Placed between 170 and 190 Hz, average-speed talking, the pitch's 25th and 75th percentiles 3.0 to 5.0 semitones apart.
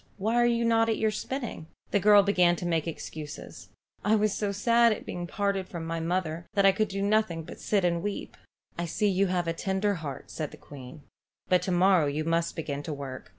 No: medium, 185 Hz; fast, 225 wpm; average, 4.0 semitones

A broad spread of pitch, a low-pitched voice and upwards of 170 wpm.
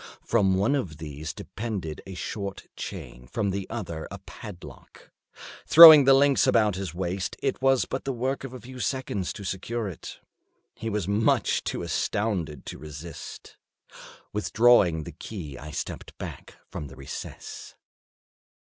No: wide, 6.5 semitones; low, 100 Hz; average, 150 wpm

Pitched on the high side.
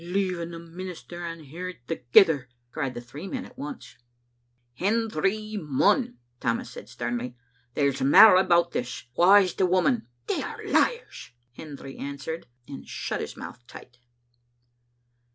No: medium, 170 Hz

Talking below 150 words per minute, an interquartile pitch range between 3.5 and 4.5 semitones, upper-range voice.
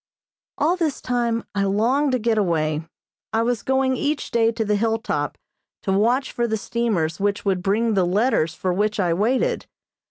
No: average, 185 wpm; average, 3.9 semitones; high, 220 Hz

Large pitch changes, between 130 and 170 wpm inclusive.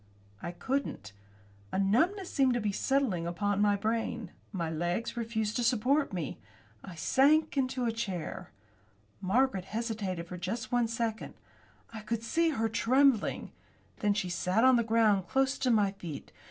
No: average, 4.7 semitones; average, 155 wpm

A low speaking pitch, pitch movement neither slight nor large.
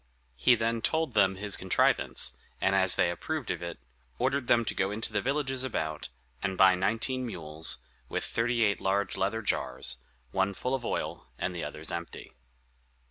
Yes: low, 100 Hz; average, 4.6 semitones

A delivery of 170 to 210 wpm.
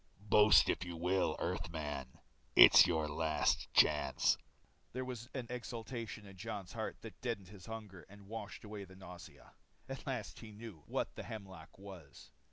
No: average, 160 wpm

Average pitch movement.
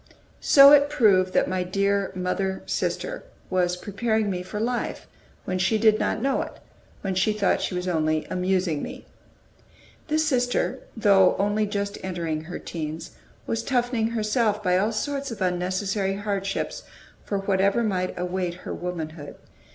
Yes: average, 3.2 semitones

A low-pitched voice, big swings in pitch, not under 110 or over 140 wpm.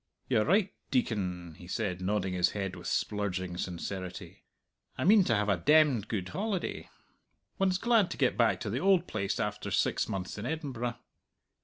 No: low, 105 Hz; wide, 8.3 semitones; average, 170 wpm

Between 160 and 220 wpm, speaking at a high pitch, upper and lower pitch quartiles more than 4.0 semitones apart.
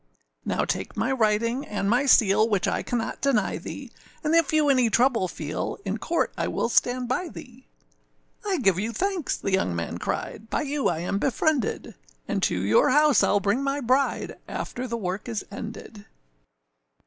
Yes: average, 180 wpm; high, 235 Hz; average, 5.3 semitones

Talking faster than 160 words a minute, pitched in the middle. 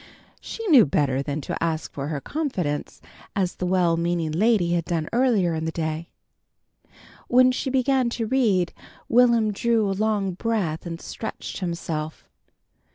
No: average, 155 wpm; medium, 180 Hz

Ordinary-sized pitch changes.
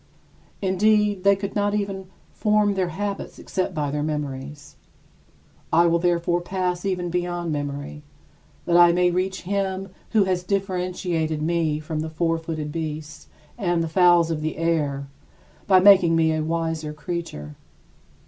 Yes: average, 3.2 semitones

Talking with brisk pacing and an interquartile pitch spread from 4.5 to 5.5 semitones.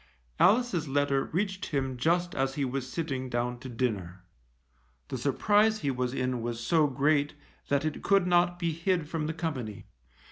No: average, 170 wpm; average, 5.1 semitones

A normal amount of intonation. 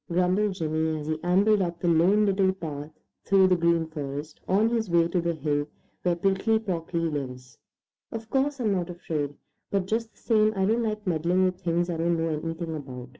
Yes: average, 3.6 semitones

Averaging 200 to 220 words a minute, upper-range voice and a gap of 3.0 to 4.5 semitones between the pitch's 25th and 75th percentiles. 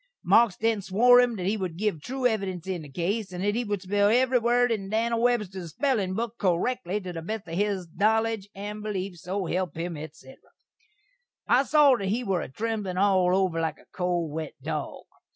Yes: fast, 205 wpm; high, 200 Hz; average, 4.0 semitones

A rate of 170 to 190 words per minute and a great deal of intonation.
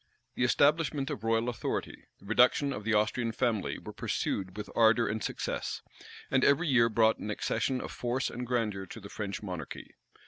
No: average, 180 wpm; average, 3.0 semitones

